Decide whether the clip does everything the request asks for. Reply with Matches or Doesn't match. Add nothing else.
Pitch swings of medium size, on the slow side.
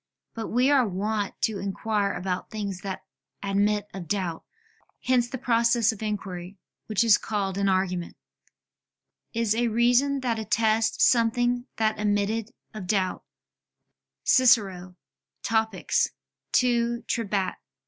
Matches